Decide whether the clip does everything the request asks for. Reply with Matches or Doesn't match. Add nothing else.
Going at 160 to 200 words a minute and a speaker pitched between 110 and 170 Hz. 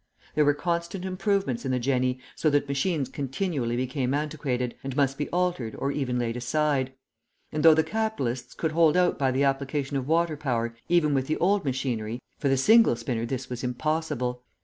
Matches